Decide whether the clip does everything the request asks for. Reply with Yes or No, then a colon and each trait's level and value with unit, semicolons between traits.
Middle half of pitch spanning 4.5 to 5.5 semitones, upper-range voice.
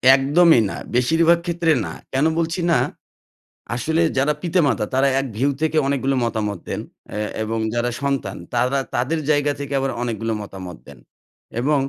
No: average, 5.2 semitones; low, 135 Hz